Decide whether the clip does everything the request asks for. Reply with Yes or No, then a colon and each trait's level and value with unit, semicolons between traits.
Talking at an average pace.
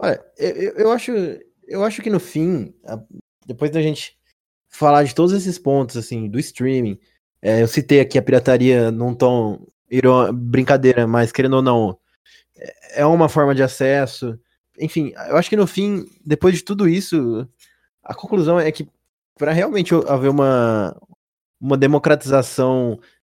Yes: average, 150 wpm